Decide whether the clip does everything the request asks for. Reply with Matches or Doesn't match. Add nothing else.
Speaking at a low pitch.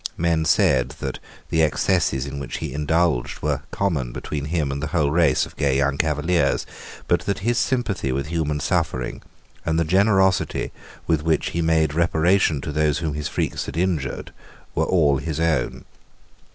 Matches